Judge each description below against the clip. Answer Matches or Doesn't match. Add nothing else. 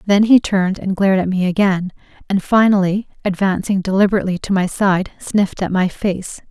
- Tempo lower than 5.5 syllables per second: Doesn't match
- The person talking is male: Doesn't match